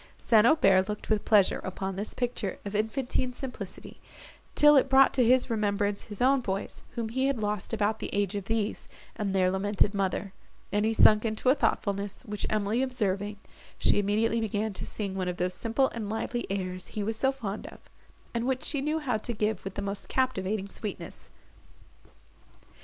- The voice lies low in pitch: No, high, 215 Hz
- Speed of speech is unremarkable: Yes, average, 185 wpm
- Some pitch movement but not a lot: Yes, average, 3.2 semitones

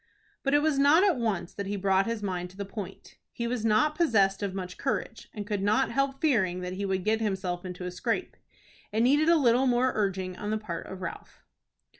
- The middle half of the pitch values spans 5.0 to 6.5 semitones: Yes, average, 5.3 semitones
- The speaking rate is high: Yes, fast, 225 wpm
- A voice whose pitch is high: Yes, high, 210 Hz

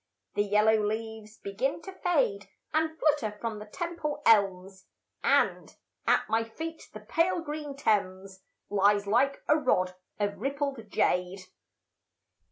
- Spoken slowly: Yes, slow, 130 wpm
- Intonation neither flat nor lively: No, wide, 6.6 semitones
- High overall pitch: Yes, high, 220 Hz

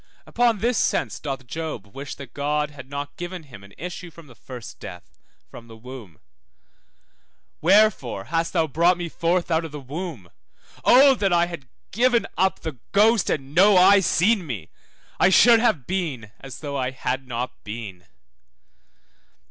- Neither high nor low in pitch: Yes, medium, 155 Hz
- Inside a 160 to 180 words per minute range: Yes, average, 165 wpm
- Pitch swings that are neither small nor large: No, wide, 6.3 semitones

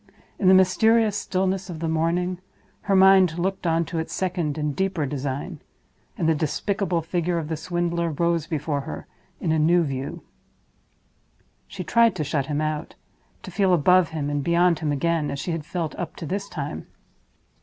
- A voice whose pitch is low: No, medium, 170 Hz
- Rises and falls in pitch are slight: No, average, 3.2 semitones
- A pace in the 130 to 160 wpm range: No, average, 180 wpm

